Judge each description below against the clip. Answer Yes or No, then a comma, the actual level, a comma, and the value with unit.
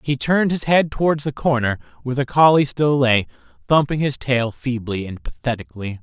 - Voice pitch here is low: Yes, low, 130 Hz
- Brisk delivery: No, average, 180 wpm